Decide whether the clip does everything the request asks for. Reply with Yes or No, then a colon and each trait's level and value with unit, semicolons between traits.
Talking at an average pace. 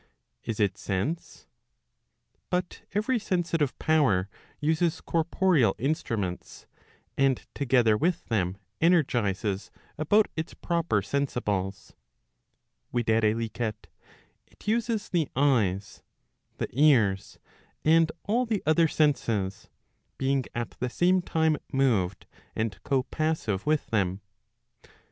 No: slow, 100 wpm